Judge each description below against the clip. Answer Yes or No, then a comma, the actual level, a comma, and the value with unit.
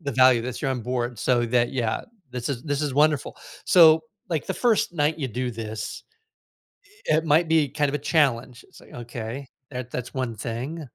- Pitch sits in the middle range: No, low, 130 Hz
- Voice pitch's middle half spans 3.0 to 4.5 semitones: Yes, average, 3.8 semitones